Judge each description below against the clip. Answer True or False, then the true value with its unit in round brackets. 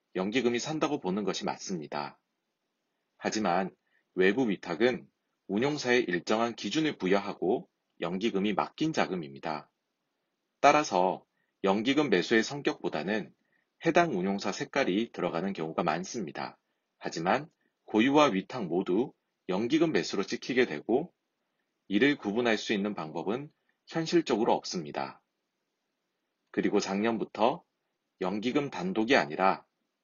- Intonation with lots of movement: True (7.0 semitones)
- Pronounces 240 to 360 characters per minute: True (275 characters per minute)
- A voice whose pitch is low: True (120 Hz)